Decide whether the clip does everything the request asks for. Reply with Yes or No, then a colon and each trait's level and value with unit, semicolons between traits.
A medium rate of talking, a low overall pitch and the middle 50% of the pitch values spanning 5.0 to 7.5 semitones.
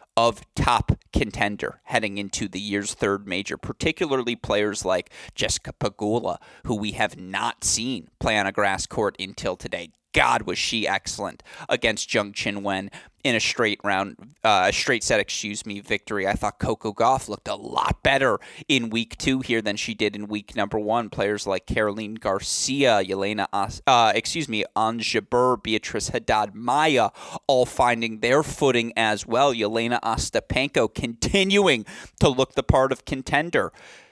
No: average, 160 wpm; low, 115 Hz; average, 3.3 semitones